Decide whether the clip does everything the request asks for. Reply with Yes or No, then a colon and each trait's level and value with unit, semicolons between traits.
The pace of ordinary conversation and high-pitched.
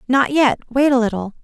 No: fast, 210 wpm; very high, 250 Hz